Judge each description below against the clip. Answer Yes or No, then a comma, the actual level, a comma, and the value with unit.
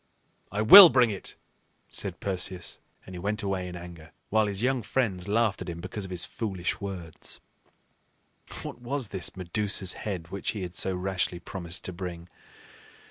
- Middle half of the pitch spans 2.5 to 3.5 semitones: Yes, average, 3.1 semitones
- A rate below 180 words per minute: Yes, average, 170 wpm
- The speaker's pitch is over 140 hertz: No, very low, 95 Hz